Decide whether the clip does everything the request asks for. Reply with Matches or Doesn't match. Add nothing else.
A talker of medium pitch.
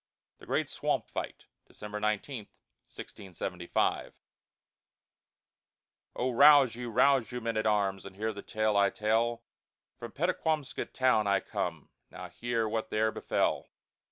Doesn't match